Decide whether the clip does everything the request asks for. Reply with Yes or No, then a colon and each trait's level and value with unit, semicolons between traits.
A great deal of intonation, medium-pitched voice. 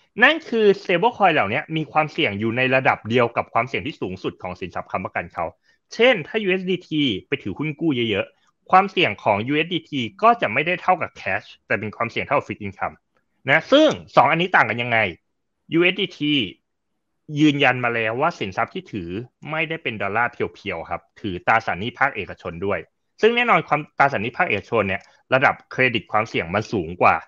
Yes: wide, 7.9 semitones; medium, 150 Hz